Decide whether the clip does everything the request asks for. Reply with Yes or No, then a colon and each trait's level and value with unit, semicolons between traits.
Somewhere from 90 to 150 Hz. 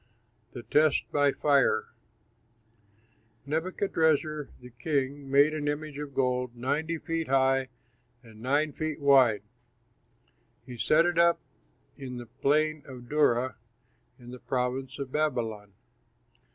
Yes: medium, 140 Hz